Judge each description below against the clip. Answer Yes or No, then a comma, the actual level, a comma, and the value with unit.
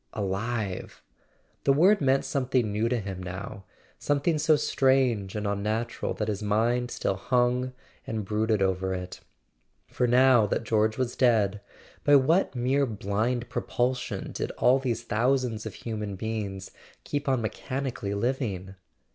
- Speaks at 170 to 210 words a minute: No, average, 140 wpm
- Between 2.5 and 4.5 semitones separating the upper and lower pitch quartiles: Yes, average, 4.0 semitones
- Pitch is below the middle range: Yes, low, 115 Hz